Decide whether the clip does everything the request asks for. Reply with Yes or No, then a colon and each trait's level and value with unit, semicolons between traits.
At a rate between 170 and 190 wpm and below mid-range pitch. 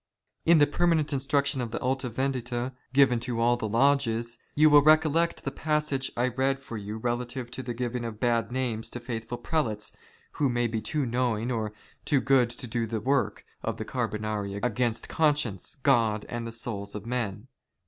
Yes: average, 185 wpm; low, 120 Hz